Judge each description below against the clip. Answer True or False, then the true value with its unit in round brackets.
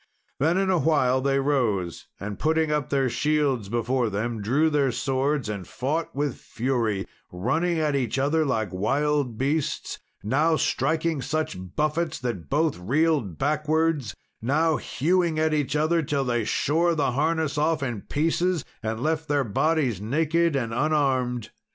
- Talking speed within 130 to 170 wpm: True (150 wpm)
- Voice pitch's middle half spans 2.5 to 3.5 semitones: False (4.4 semitones)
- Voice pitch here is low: False (145 Hz)